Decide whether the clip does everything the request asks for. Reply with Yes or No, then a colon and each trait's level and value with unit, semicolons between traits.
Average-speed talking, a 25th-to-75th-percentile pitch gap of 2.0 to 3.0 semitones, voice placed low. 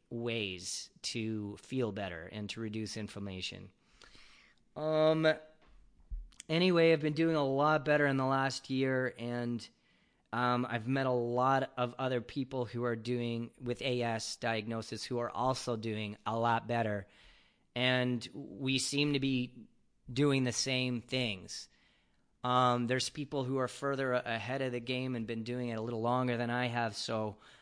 Yes: average, 155 wpm; narrow, 2.5 semitones; low, 125 Hz